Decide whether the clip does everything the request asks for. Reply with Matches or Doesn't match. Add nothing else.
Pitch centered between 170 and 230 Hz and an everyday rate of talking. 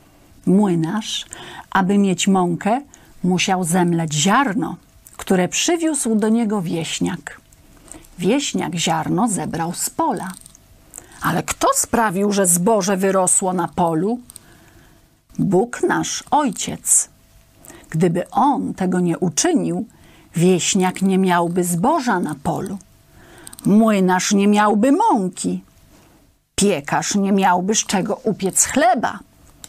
Doesn't match